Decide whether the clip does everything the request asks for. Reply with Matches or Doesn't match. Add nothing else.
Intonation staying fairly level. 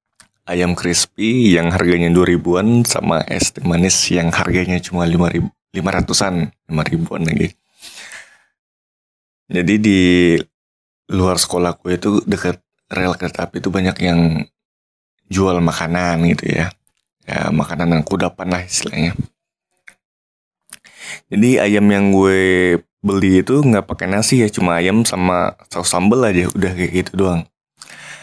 Matches